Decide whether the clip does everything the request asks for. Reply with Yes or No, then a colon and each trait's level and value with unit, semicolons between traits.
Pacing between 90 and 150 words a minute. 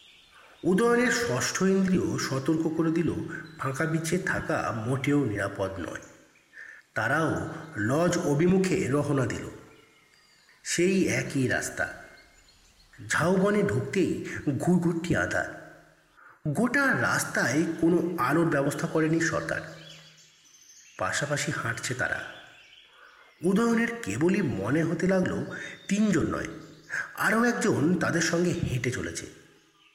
Yes: average, 95 wpm